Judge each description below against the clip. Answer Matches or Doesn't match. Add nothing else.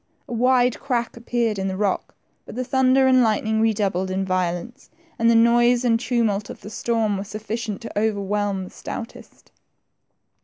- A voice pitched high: Matches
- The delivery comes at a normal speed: Matches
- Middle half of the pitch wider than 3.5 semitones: Doesn't match